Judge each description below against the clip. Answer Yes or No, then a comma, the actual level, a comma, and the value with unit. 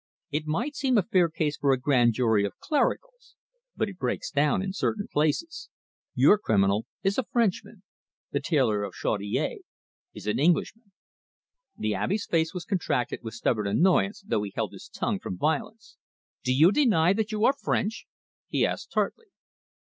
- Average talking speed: Yes, average, 170 wpm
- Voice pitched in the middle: Yes, medium, 165 Hz